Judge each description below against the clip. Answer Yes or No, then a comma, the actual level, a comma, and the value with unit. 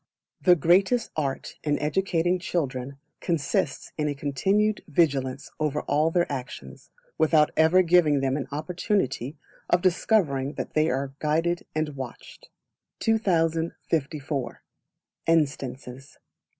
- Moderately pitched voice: Yes, medium, 155 Hz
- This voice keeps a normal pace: No, slow, 110 wpm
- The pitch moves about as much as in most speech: Yes, average, 4.0 semitones